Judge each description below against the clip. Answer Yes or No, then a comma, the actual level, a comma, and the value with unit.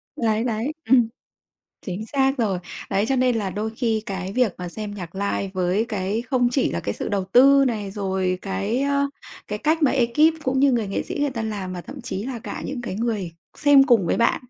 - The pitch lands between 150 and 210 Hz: No, high, 220 Hz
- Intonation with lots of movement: No, average, 4.9 semitones